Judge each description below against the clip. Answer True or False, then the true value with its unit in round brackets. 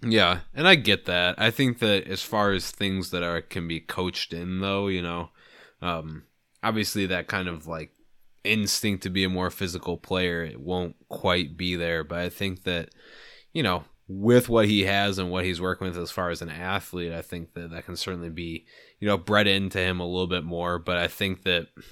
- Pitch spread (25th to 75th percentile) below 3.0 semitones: True (2.4 semitones)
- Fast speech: True (215 wpm)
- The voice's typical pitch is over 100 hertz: False (90 Hz)